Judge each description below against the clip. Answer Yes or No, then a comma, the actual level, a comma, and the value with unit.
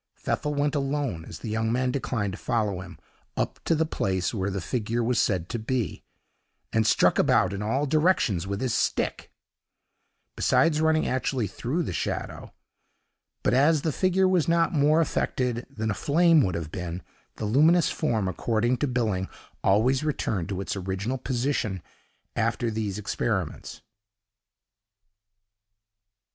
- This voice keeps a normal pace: Yes, average, 150 wpm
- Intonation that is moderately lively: No, wide, 6.6 semitones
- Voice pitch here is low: Yes, low, 120 Hz